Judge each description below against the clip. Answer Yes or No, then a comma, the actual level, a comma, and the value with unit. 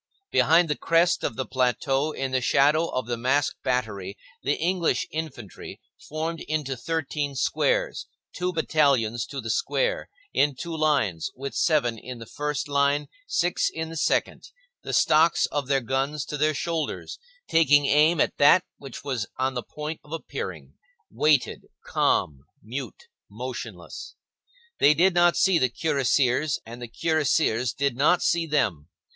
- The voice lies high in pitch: No, medium, 145 Hz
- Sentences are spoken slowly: No, average, 150 wpm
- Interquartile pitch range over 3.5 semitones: Yes, average, 4.0 semitones